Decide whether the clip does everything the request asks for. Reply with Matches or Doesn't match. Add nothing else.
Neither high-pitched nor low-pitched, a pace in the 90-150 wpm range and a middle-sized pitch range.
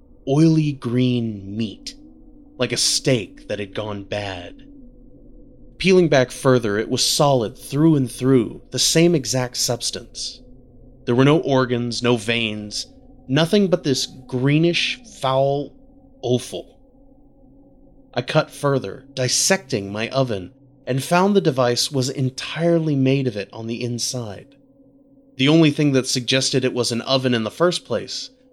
Doesn't match